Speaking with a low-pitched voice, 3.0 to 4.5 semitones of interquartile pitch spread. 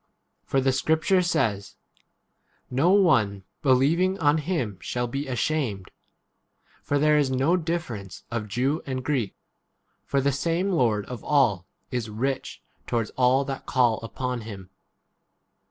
No: low, 130 Hz; average, 5.0 semitones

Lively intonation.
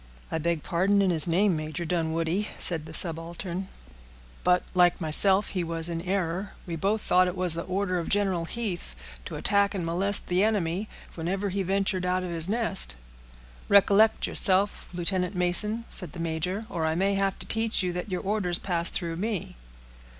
No: average, 2.8 semitones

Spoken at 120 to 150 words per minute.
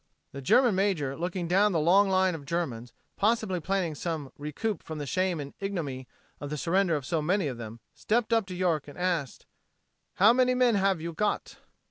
No: average, 195 wpm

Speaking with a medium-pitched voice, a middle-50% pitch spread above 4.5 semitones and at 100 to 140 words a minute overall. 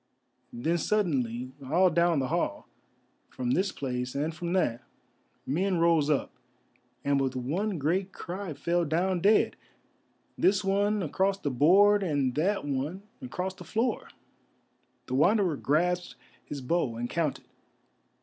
Yes: medium, 170 Hz; wide, 5.5 semitones; slow, 135 wpm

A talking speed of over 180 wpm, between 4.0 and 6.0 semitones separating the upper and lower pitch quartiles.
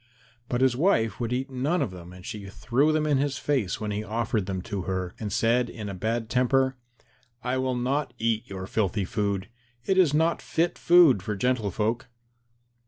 Yes: average, 195 wpm; average, 4.6 semitones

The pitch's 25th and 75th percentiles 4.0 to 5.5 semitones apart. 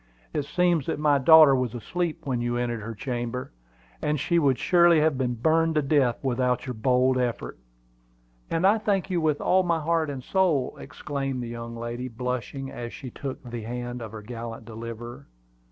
Yes: average, 4.5 semitones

